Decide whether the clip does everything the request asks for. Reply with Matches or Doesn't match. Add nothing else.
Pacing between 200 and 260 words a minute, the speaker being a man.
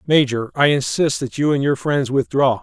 Matches